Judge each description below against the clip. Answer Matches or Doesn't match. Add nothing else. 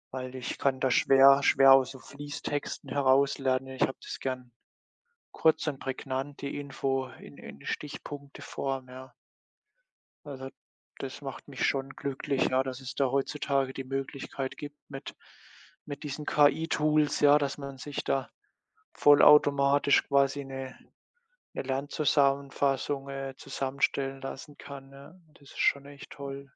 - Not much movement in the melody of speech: Matches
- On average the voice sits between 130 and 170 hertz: Matches